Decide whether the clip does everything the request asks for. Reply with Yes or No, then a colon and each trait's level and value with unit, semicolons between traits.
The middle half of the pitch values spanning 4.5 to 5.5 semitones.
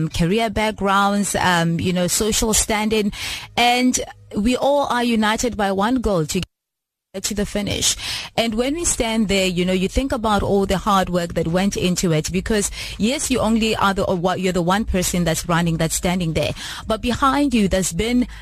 No: average, 3.6 semitones